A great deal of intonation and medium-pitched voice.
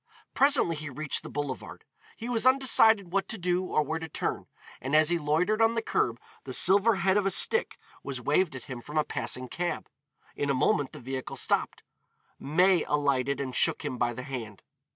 Yes: wide, 6.4 semitones; medium, 155 Hz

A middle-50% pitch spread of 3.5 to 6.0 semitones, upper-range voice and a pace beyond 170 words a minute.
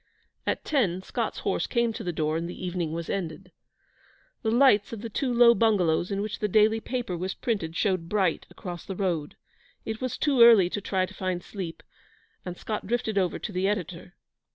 Yes: average, 4.0 semitones; high, 195 Hz; average, 200 wpm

